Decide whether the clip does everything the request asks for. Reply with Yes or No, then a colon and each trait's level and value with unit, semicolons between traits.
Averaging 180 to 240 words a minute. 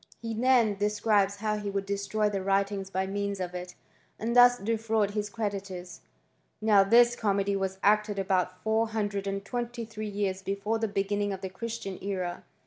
No: average, 165 wpm